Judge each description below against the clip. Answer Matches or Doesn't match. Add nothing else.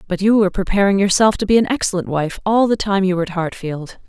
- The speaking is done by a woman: Matches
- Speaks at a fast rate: Matches